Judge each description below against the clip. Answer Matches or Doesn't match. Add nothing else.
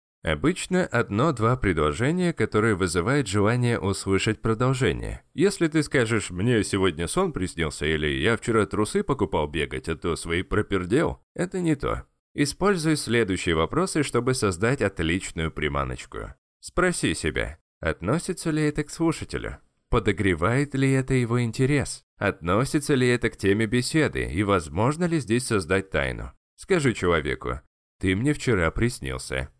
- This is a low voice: Matches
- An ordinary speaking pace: Matches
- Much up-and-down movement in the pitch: Matches